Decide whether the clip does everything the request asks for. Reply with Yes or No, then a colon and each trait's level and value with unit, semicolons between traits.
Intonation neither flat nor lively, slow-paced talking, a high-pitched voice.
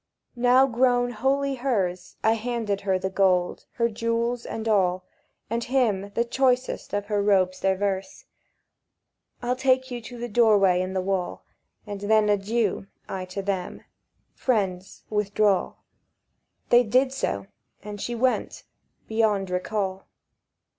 Yes: average, 3.9 semitones; slow, 125 wpm; high, 210 Hz